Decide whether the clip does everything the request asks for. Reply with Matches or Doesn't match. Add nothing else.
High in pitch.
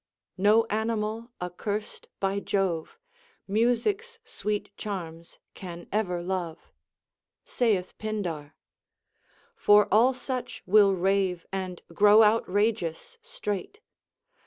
Matches